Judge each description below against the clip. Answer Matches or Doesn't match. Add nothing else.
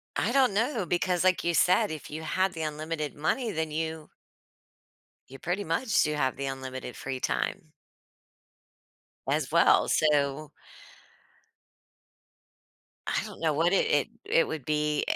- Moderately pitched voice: Matches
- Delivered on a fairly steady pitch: Doesn't match